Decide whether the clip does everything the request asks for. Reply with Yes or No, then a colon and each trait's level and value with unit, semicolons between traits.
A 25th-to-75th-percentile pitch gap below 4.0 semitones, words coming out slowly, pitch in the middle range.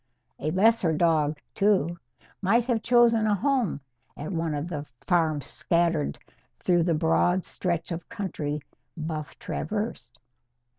No: average, 5.0 semitones; slow, 130 wpm; medium, 170 Hz